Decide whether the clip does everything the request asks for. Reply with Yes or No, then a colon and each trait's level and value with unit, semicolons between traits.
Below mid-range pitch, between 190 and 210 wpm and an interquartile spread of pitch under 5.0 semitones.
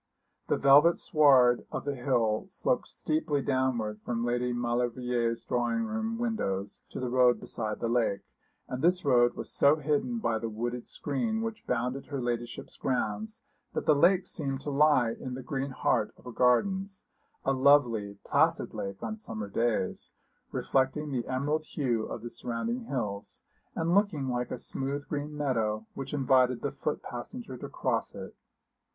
No: low, 130 Hz; average, 165 wpm; average, 3.9 semitones